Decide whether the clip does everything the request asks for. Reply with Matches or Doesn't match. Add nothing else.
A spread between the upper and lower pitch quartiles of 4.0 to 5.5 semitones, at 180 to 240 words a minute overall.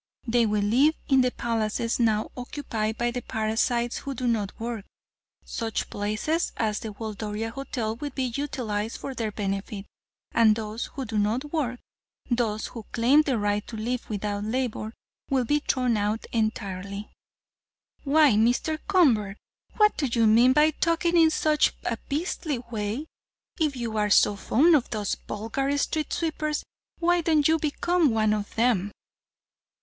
Doesn't match